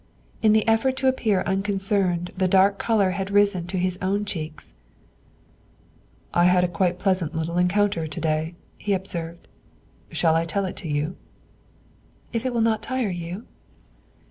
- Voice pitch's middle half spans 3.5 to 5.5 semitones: No, average, 3.1 semitones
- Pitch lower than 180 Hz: No, medium, 185 Hz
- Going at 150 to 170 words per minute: Yes, average, 160 wpm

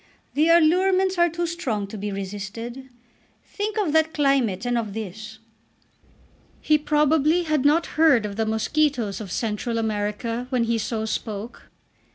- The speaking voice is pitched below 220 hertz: No, high, 245 Hz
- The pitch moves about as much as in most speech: No, wide, 6.3 semitones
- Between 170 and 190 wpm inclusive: No, average, 150 wpm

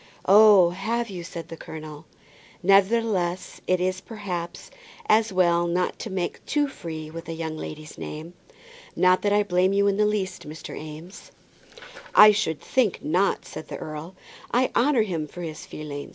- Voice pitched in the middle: Yes, medium, 180 Hz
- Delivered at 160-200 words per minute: Yes, average, 165 wpm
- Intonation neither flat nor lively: Yes, average, 4.2 semitones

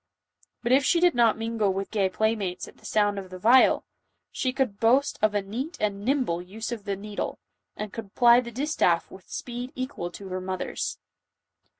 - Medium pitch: No, high, 215 Hz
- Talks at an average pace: Yes, average, 195 wpm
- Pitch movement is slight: No, average, 4.0 semitones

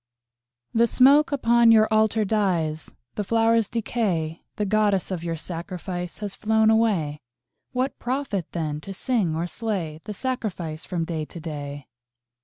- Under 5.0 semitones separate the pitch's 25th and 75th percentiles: No, wide, 5.5 semitones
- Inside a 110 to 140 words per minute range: No, average, 150 wpm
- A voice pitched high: Yes, high, 200 Hz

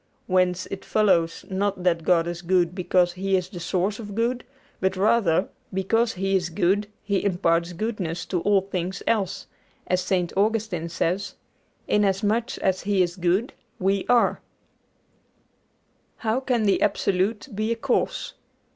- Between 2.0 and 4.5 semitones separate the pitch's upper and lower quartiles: Yes, average, 2.7 semitones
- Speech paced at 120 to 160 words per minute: Yes, average, 145 wpm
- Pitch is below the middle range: No, high, 190 Hz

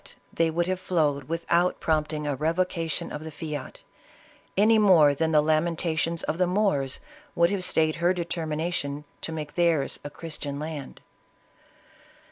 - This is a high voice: No, medium, 160 Hz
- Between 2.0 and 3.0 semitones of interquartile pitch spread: Yes, narrow, 2.4 semitones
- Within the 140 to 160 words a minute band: Yes, average, 150 wpm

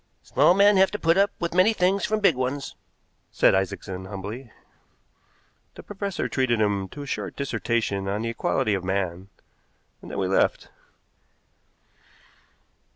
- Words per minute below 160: Yes, average, 150 wpm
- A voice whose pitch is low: Yes, low, 125 Hz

